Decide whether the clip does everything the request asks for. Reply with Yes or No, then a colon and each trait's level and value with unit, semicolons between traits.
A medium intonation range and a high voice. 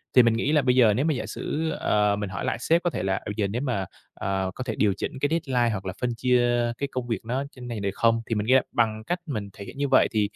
No: average, 4.0 semitones; low, 120 Hz